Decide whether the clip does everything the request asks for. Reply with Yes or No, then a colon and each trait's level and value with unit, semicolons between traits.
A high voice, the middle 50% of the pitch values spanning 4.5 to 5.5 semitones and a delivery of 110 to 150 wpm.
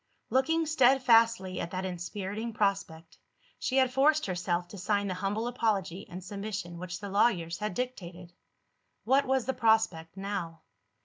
Yes: high, 200 Hz; average, 4.8 semitones; average, 145 wpm